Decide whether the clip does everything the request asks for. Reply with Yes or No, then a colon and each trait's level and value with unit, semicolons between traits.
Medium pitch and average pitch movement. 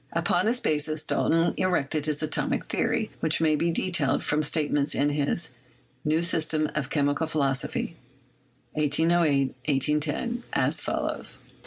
No: medium, 155 Hz; narrow, 2.2 semitones